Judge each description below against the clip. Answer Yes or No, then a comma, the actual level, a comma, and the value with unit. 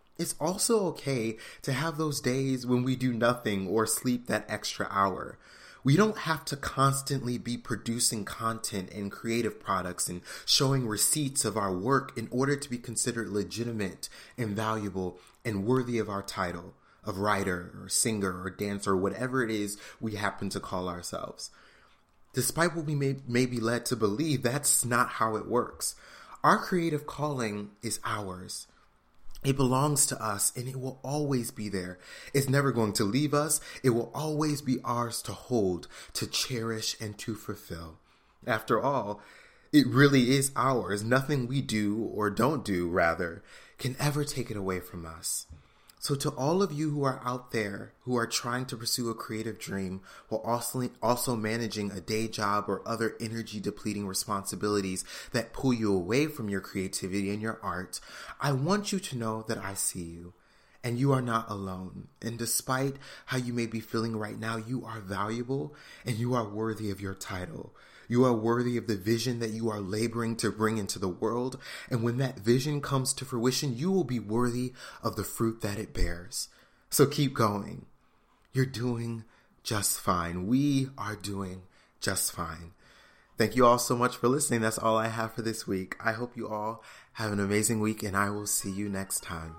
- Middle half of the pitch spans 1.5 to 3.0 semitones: No, average, 4.0 semitones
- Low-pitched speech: Yes, low, 115 Hz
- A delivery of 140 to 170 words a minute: No, average, 185 wpm